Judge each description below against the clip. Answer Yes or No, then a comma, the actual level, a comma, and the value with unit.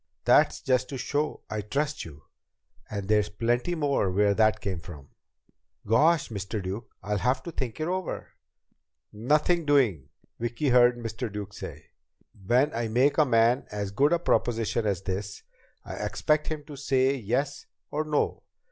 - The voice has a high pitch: No, low, 120 Hz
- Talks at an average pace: Yes, average, 160 wpm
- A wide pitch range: Yes, wide, 5.7 semitones